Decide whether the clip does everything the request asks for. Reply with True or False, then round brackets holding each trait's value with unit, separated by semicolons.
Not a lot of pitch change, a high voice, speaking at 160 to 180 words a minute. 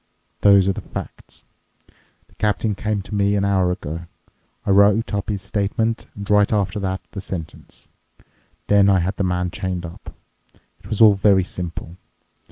False (1.9 semitones; 100 Hz; 170 wpm)